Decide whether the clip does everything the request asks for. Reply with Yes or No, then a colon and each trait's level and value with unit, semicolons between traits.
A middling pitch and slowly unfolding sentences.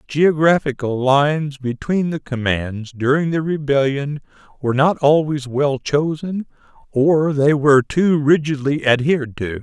Yes: medium, 145 Hz; slow, 125 wpm